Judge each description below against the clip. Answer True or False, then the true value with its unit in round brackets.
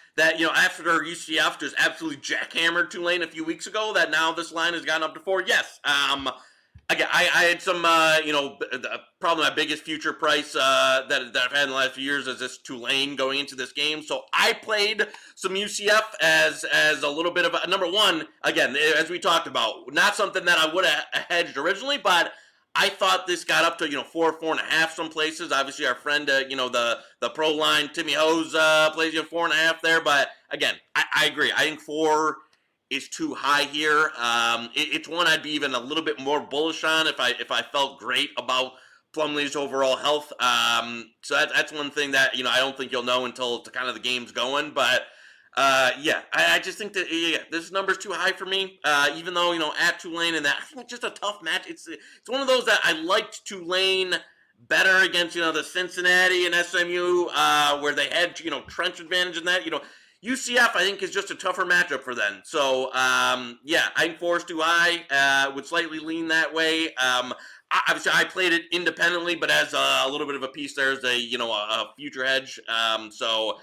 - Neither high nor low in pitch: True (155 Hz)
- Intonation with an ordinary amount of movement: True (4.0 semitones)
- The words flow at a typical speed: False (230 wpm)